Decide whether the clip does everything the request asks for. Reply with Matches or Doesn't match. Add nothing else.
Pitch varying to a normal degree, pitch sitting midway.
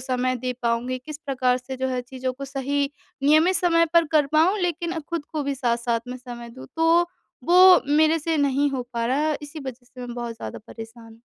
Doesn't match